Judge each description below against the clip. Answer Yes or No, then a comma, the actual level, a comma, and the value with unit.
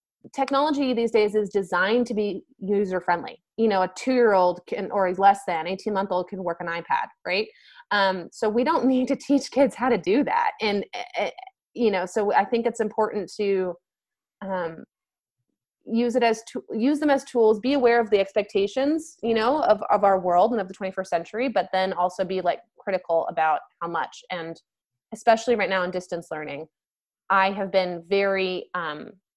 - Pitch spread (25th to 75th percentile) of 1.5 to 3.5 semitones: No, average, 4.3 semitones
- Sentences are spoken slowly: No, average, 185 wpm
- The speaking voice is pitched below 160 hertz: No, high, 205 Hz